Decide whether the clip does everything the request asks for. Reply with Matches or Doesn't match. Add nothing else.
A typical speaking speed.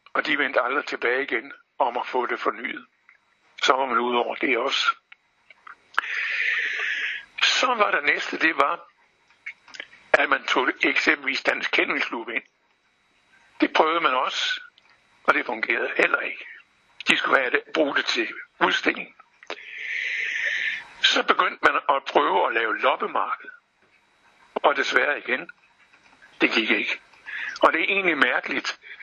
Doesn't match